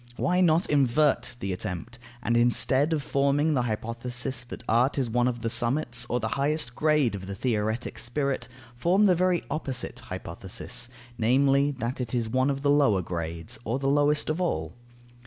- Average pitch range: Yes, average, 3.8 semitones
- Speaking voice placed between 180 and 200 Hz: No, low, 125 Hz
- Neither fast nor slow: Yes, average, 175 wpm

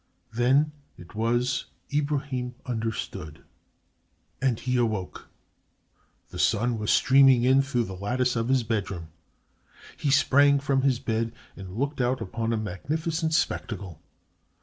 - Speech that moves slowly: Yes, slow, 125 wpm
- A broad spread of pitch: No, average, 3.8 semitones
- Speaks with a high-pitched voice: No, low, 120 Hz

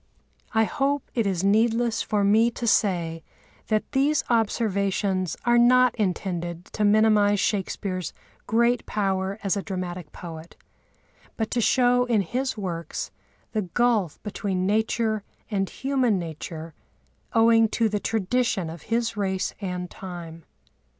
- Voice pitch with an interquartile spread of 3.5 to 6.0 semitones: Yes, average, 3.9 semitones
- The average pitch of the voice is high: Yes, high, 205 Hz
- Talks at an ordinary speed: No, slow, 130 wpm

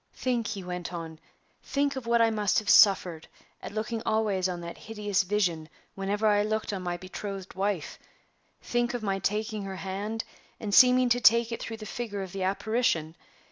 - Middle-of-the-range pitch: No, high, 205 Hz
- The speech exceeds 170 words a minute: Yes, average, 185 wpm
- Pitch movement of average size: Yes, average, 3.0 semitones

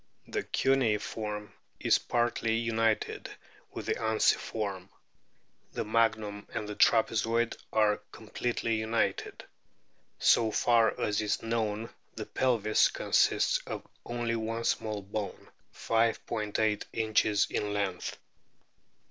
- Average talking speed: No, slow, 110 wpm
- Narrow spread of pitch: Yes, narrow, 1.6 semitones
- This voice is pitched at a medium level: No, low, 110 Hz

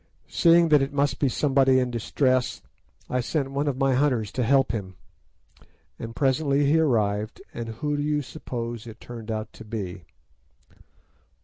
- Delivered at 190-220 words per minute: No, average, 165 wpm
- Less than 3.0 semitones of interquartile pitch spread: No, average, 4.0 semitones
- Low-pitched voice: Yes, low, 130 Hz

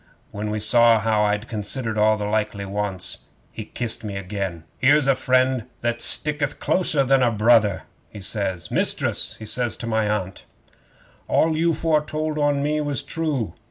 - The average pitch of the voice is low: Yes, low, 115 Hz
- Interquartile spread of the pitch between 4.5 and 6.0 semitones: Yes, average, 5.1 semitones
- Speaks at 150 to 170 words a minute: Yes, average, 165 wpm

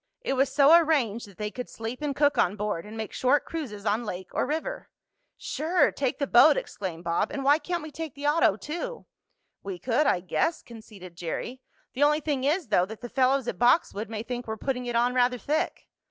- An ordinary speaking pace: No, fast, 215 wpm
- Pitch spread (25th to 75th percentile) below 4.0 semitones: No, wide, 5.5 semitones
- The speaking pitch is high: Yes, very high, 250 Hz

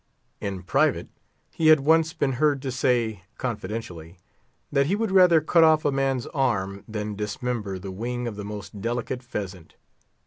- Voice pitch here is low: Yes, low, 120 Hz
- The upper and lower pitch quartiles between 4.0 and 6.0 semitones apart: Yes, wide, 5.6 semitones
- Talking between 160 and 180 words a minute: Yes, average, 165 wpm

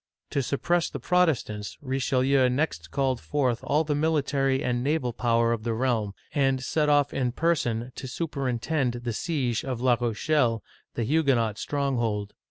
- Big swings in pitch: No, average, 3.6 semitones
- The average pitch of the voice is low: Yes, low, 130 Hz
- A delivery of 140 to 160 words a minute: Yes, average, 155 wpm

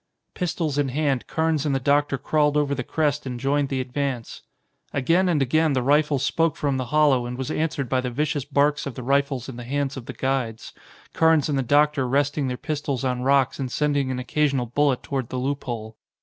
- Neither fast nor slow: No, fast, 210 wpm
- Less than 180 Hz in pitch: Yes, medium, 140 Hz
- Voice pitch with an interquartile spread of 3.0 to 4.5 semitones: No, narrow, 2.4 semitones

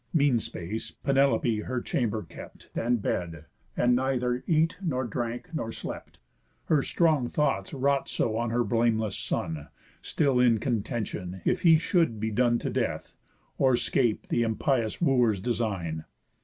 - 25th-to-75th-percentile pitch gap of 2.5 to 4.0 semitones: Yes, average, 3.7 semitones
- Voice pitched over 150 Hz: No, low, 120 Hz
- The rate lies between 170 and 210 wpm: No, average, 145 wpm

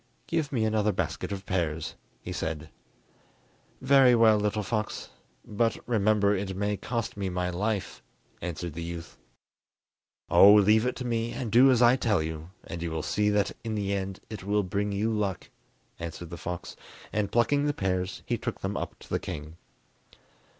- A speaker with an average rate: Yes, average, 180 wpm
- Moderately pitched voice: No, low, 100 Hz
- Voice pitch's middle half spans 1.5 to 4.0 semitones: Yes, average, 3.7 semitones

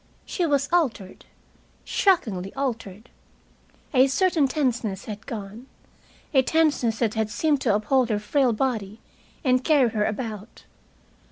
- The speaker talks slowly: Yes, slow, 125 wpm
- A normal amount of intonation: Yes, average, 4.5 semitones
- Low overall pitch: No, high, 245 Hz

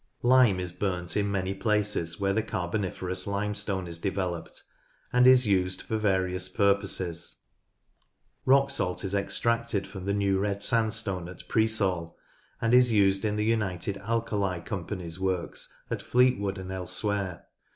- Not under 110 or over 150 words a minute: Yes, average, 145 wpm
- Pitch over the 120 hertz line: No, low, 100 Hz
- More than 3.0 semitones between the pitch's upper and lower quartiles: No, average, 2.7 semitones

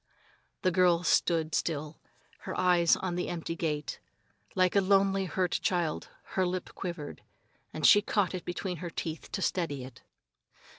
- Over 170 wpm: No, average, 155 wpm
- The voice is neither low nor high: Yes, medium, 175 Hz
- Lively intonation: No, narrow, 2.4 semitones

